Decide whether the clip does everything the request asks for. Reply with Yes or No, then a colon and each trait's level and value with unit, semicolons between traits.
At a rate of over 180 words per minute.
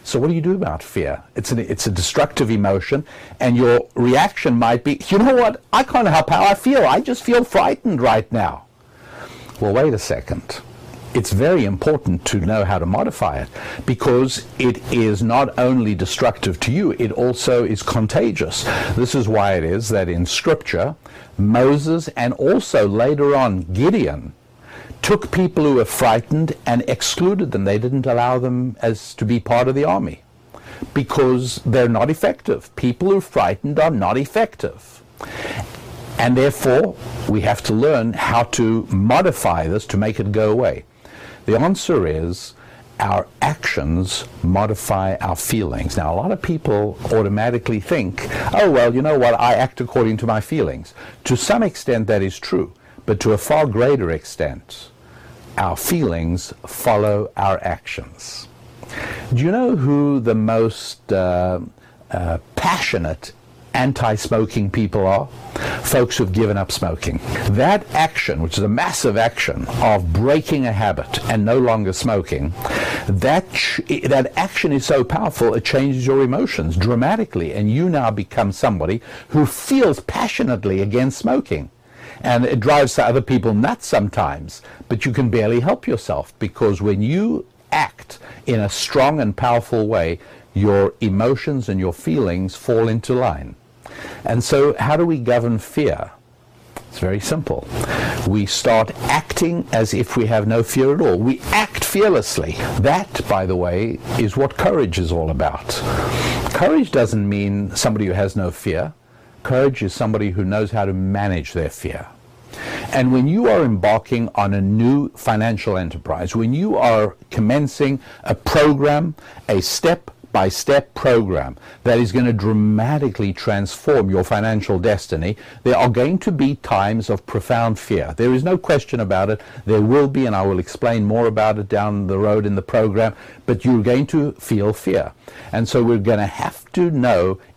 No: average, 160 wpm